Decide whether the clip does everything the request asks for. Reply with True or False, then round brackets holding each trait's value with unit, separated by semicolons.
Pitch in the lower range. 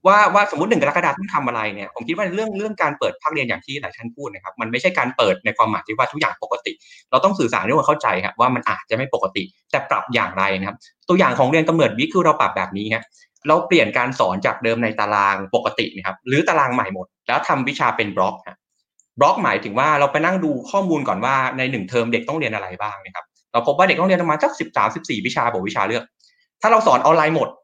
False (150 Hz)